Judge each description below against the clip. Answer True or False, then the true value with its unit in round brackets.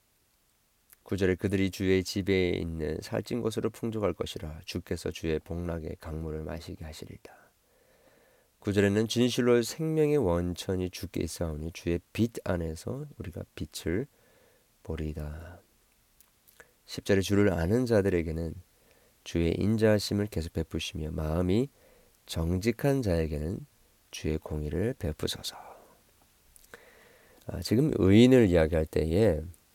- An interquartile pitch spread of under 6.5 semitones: True (5.3 semitones)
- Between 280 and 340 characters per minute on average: False (260 characters per minute)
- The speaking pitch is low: True (90 Hz)